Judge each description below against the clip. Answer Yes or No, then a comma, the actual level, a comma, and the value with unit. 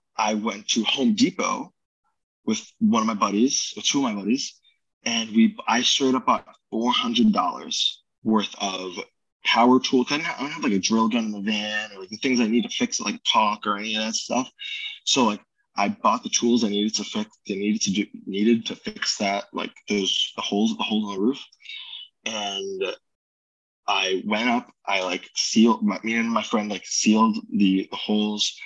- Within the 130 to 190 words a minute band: No, fast, 205 wpm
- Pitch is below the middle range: Yes, low, 120 Hz